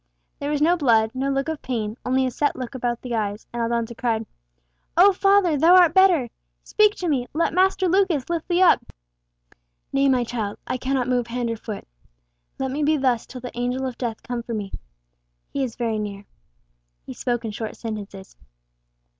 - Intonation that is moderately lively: Yes, average, 4.8 semitones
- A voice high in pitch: Yes, very high, 255 Hz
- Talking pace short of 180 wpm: No, average, 195 wpm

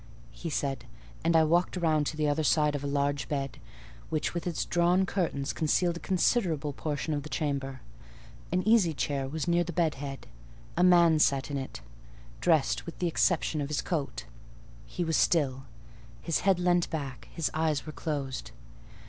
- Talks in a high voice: No, medium, 155 Hz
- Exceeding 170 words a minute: Yes, average, 180 wpm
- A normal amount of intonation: Yes, average, 3.4 semitones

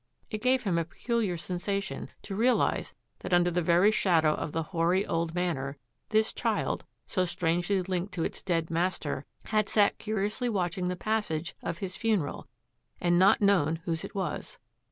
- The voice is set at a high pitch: No, medium, 180 Hz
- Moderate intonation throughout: Yes, average, 3.4 semitones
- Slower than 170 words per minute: No, average, 175 wpm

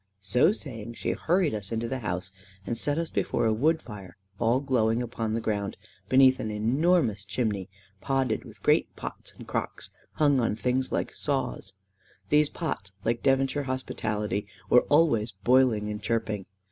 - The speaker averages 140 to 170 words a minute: Yes, average, 160 wpm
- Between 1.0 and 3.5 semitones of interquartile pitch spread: No, average, 4.2 semitones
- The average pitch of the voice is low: Yes, low, 115 Hz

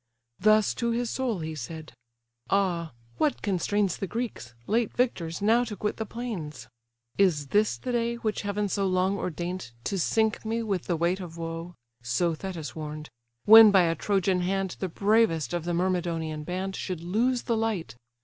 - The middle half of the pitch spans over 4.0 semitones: Yes, average, 4.5 semitones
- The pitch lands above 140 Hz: Yes, high, 190 Hz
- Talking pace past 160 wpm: Yes, average, 180 wpm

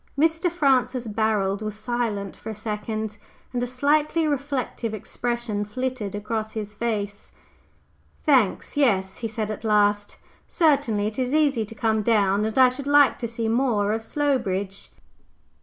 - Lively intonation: No, average, 3.7 semitones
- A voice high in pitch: Yes, high, 225 Hz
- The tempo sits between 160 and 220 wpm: No, average, 150 wpm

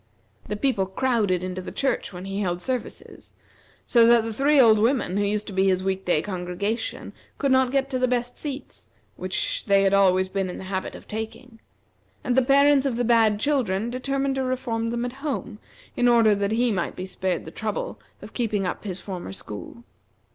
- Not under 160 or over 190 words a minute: No, fast, 205 wpm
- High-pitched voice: Yes, high, 220 Hz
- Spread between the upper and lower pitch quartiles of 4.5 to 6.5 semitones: Yes, average, 4.9 semitones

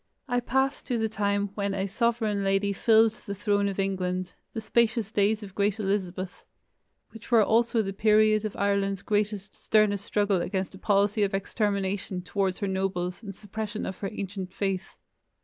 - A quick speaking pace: No, average, 170 wpm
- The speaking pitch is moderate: No, high, 200 Hz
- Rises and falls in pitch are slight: Yes, narrow, 1.9 semitones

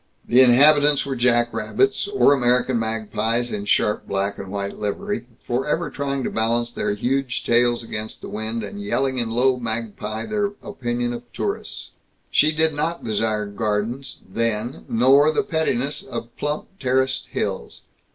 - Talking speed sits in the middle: Yes, average, 150 wpm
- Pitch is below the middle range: Yes, low, 120 Hz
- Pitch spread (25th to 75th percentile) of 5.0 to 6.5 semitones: No, average, 3.7 semitones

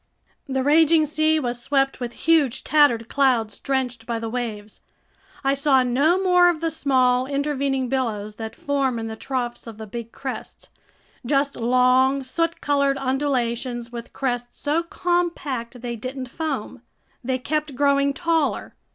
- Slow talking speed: No, average, 150 wpm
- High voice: Yes, very high, 265 Hz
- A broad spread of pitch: No, average, 3.2 semitones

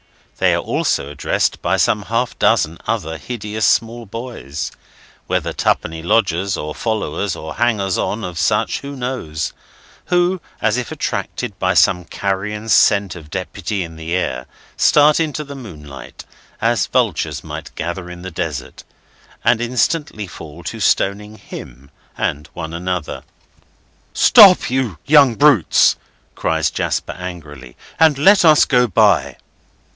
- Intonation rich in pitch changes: Yes, wide, 6.7 semitones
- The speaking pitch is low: Yes, low, 100 Hz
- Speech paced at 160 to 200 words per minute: No, slow, 135 wpm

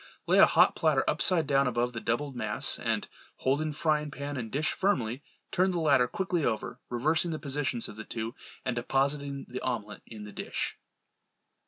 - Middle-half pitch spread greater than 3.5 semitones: Yes, average, 4.1 semitones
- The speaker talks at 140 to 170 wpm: No, average, 180 wpm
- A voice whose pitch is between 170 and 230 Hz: No, low, 135 Hz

